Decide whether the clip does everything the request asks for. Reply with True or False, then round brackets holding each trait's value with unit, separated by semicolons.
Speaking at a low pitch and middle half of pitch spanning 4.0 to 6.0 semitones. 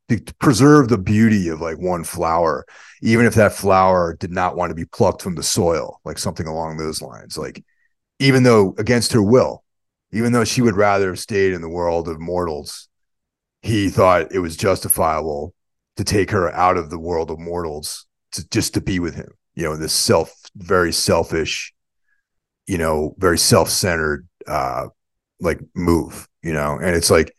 True (90 Hz; 4.3 semitones)